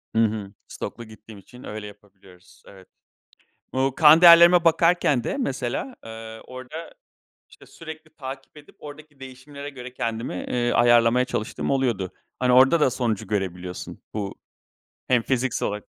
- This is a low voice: Yes, low, 125 Hz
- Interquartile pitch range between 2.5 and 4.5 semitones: No, average, 4.9 semitones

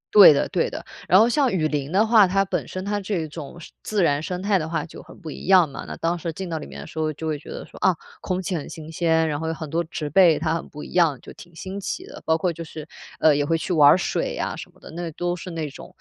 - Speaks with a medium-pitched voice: Yes, medium, 165 Hz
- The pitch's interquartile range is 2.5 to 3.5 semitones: Yes, average, 3.1 semitones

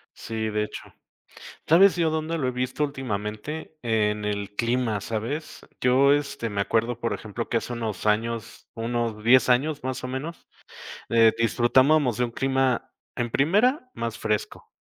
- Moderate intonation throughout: Yes, average, 3.7 semitones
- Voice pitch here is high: No, low, 120 Hz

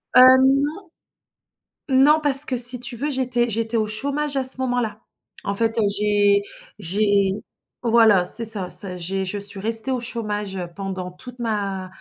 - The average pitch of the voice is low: No, high, 225 Hz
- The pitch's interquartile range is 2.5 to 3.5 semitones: No, average, 4.0 semitones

